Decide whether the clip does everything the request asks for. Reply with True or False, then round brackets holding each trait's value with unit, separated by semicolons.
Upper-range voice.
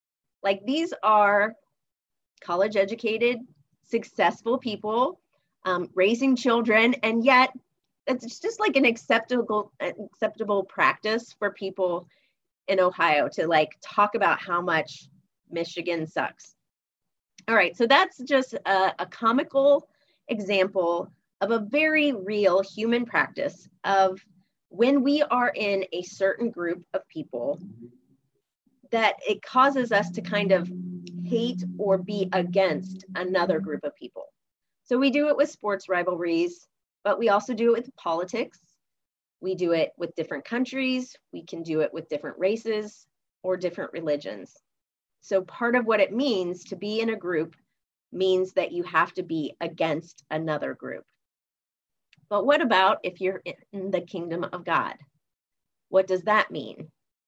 True (195 Hz)